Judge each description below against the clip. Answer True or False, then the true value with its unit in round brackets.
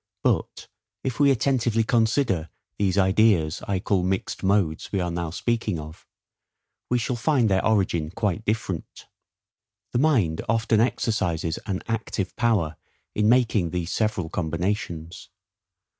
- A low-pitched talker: True (100 Hz)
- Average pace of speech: False (130 wpm)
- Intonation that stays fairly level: False (4.7 semitones)